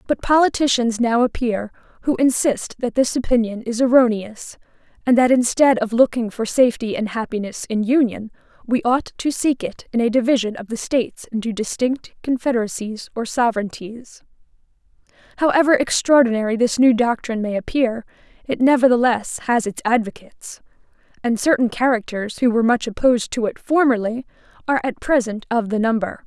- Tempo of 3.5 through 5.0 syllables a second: No, 5.5 syllables/s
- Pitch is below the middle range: No, high, 240 Hz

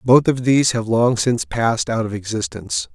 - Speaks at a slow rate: No, fast, 205 wpm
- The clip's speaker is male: Yes, male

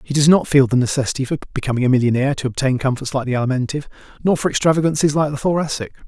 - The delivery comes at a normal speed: No, fast, 215 wpm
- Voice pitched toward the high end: No, medium, 140 Hz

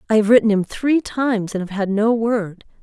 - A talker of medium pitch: No, high, 220 Hz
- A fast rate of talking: Yes, fast, 235 wpm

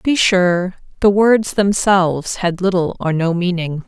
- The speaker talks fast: No, average, 170 wpm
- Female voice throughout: Yes, female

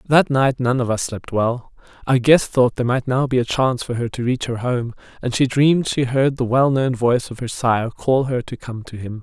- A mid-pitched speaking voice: No, low, 125 Hz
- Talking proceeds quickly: Yes, fast, 255 wpm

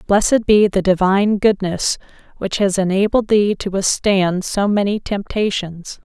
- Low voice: No, high, 200 Hz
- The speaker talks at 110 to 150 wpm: Yes, average, 140 wpm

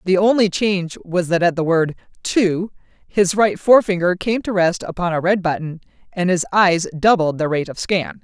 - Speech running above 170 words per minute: Yes, average, 195 wpm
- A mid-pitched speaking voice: Yes, medium, 180 Hz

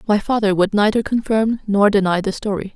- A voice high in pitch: Yes, high, 205 Hz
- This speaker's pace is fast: No, average, 195 wpm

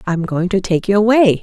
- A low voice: No, high, 195 Hz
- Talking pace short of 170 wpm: No, fast, 250 wpm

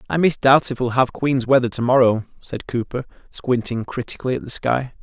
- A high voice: No, low, 125 Hz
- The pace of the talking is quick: No, average, 180 wpm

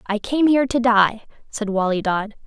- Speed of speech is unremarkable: Yes, average, 195 wpm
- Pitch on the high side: Yes, high, 225 Hz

